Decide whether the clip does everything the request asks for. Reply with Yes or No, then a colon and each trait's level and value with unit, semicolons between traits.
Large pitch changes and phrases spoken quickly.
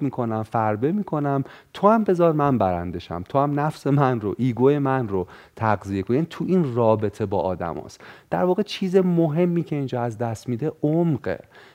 Yes: wide, 7.1 semitones; fast, 175 wpm